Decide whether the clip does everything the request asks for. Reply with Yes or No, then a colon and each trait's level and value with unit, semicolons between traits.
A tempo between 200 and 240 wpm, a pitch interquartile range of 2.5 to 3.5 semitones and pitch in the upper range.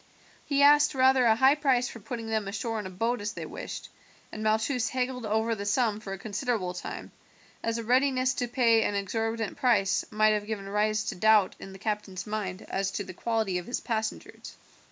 Yes: fast, 205 wpm; average, 3.2 semitones; high, 220 Hz